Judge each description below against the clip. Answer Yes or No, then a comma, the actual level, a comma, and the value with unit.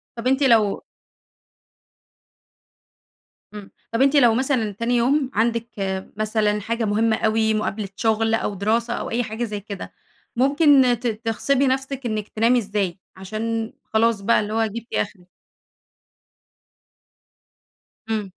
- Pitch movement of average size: No, narrow, 2.2 semitones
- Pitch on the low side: No, high, 225 Hz